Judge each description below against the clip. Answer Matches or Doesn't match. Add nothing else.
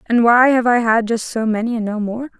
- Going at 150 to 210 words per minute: Doesn't match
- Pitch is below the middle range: Doesn't match